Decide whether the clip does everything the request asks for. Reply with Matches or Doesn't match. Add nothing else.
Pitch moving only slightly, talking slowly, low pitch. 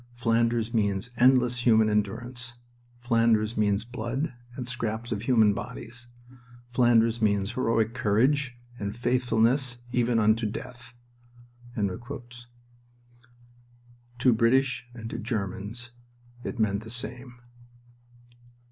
Matches